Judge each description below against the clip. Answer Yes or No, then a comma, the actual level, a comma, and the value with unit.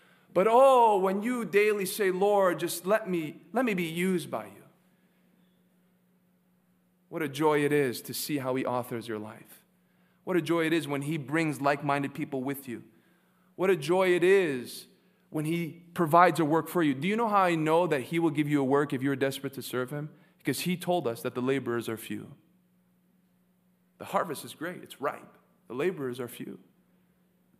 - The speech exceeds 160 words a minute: Yes, average, 200 wpm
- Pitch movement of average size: Yes, average, 4.1 semitones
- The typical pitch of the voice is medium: Yes, medium, 175 Hz